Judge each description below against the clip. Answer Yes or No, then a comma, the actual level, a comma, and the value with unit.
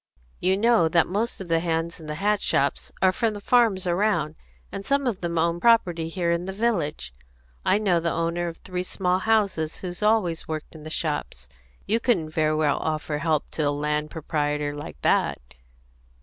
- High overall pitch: No, medium, 170 Hz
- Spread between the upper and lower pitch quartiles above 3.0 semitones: Yes, average, 4.2 semitones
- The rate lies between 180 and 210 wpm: Yes, average, 190 wpm